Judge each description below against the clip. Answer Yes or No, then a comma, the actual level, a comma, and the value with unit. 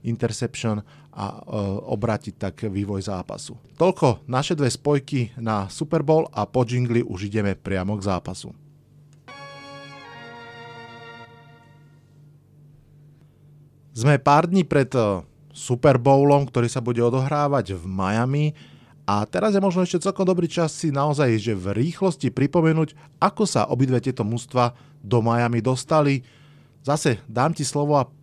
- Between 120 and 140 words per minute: Yes, average, 130 wpm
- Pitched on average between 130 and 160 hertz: Yes, low, 135 Hz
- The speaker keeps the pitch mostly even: No, average, 4.0 semitones